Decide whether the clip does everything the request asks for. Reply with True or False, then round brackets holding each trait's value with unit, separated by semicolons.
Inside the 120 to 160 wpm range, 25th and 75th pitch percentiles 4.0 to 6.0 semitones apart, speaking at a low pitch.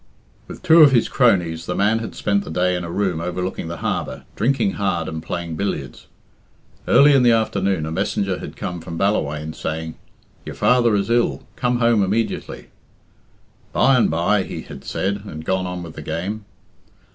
False (180 wpm; 5.1 semitones; 95 Hz)